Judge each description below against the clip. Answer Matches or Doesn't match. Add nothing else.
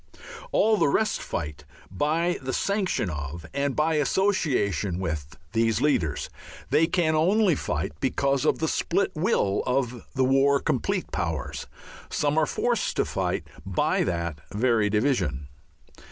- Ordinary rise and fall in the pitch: Doesn't match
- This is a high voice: Doesn't match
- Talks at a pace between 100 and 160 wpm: Matches